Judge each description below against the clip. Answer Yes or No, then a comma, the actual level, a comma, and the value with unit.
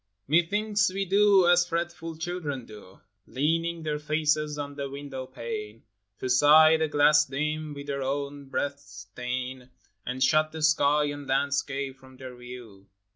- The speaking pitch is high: No, medium, 145 Hz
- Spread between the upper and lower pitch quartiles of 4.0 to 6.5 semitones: No, average, 3.2 semitones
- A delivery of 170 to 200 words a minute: No, average, 150 wpm